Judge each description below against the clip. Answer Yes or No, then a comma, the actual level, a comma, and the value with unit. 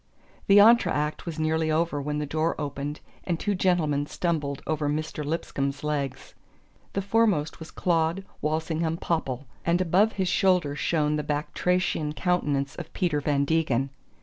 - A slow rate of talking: No, average, 150 wpm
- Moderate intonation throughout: Yes, average, 3.0 semitones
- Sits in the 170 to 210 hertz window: No, medium, 155 Hz